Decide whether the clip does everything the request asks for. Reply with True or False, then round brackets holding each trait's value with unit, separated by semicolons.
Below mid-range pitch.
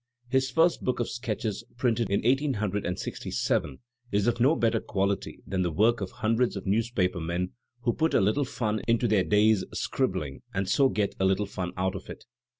True (105 Hz)